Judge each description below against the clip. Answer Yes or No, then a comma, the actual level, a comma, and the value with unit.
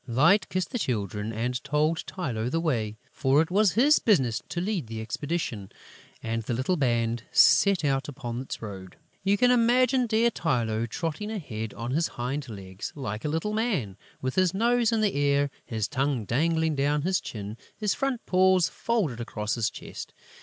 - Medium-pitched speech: Yes, medium, 145 Hz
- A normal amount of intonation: No, wide, 8.4 semitones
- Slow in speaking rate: No, average, 180 wpm